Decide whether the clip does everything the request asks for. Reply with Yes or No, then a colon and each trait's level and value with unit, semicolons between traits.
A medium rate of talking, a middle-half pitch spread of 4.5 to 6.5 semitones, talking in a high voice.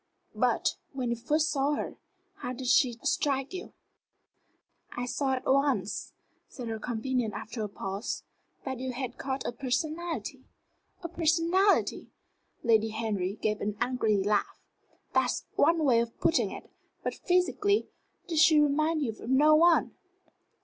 Yes: average, 145 wpm; average, 5.2 semitones; very high, 265 Hz